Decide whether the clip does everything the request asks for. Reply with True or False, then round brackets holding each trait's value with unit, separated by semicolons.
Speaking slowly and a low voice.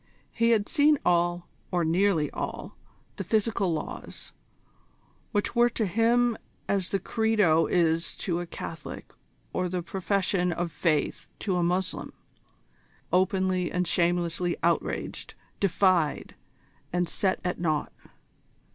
False (120 wpm; 180 Hz)